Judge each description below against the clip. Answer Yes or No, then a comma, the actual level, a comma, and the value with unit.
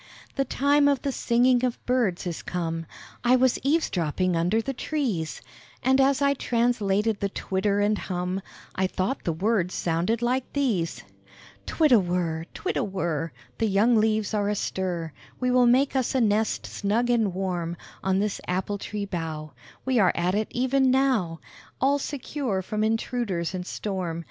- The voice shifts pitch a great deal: Yes, wide, 5.7 semitones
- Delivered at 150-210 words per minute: Yes, average, 170 wpm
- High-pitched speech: Yes, high, 210 Hz